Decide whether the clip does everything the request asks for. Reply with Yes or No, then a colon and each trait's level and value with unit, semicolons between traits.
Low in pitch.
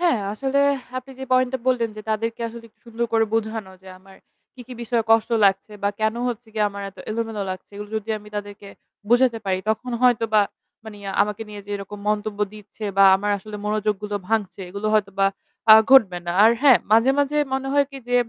No: high, 220 Hz